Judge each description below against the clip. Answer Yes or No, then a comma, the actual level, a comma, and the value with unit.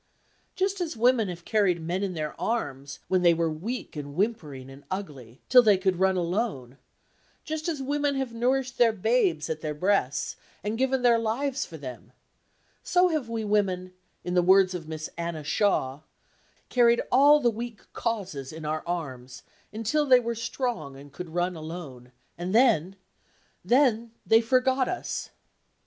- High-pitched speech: Yes, high, 195 Hz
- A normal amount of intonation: No, wide, 7.3 semitones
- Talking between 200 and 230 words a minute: No, average, 160 wpm